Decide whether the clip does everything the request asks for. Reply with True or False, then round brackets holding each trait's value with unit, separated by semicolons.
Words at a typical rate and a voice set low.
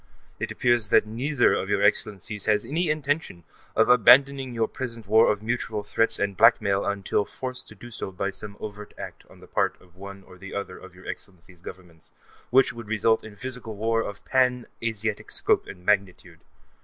True (190 wpm; 110 Hz)